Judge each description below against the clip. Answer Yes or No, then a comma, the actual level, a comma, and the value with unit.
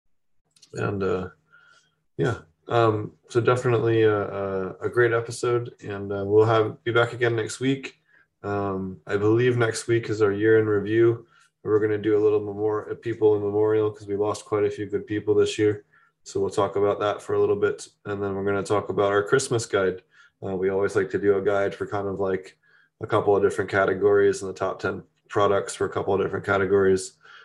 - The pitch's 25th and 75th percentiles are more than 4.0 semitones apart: No, average, 2.8 semitones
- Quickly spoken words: Yes, fast, 215 wpm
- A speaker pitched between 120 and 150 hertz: No, low, 105 Hz